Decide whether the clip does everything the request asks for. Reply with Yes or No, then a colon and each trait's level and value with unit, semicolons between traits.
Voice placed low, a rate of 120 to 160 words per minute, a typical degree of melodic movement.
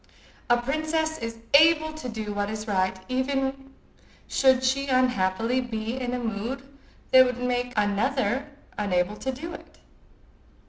No: very high, 250 Hz; average, 140 wpm; average, 3.7 semitones